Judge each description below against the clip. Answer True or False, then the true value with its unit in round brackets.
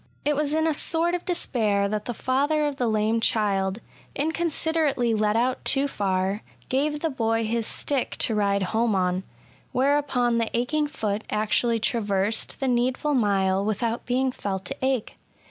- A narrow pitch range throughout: False (5.1 semitones)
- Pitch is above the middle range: True (235 Hz)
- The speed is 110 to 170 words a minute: True (165 wpm)